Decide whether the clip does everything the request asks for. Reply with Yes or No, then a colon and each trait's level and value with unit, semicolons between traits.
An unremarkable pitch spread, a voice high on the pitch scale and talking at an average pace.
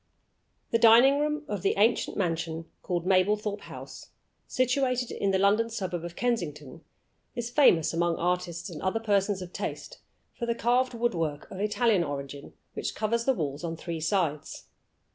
No: wide, 5.7 semitones; high, 195 Hz; average, 160 wpm